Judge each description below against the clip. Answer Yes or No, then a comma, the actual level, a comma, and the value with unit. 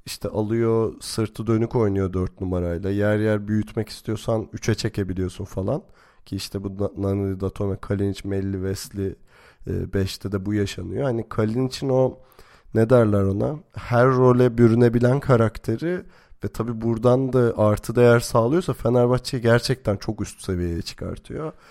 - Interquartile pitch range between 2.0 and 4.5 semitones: Yes, average, 3.5 semitones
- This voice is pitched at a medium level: No, low, 110 Hz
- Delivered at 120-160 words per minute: Yes, fast, 140 wpm